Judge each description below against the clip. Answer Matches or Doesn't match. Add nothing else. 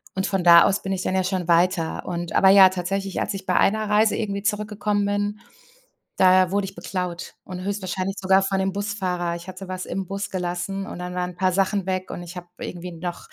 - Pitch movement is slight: Matches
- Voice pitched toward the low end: Doesn't match